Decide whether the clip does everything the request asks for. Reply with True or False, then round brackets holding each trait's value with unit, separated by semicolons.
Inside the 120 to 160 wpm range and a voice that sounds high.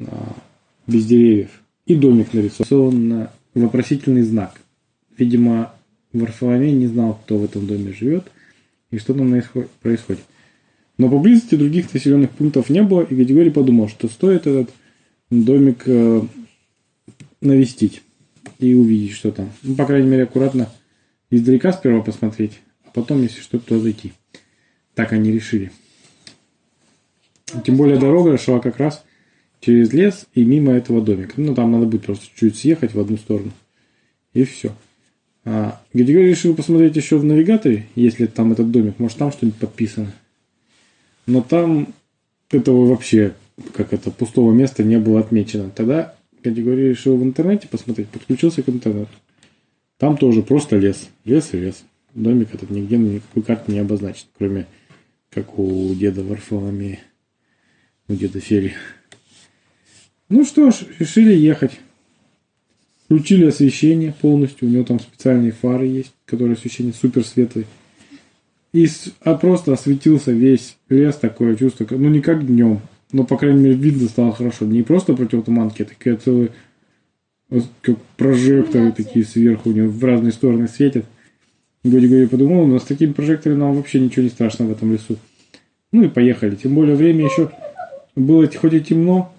False (145 wpm; 120 Hz)